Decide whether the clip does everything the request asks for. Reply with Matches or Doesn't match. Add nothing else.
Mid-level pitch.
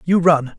Matches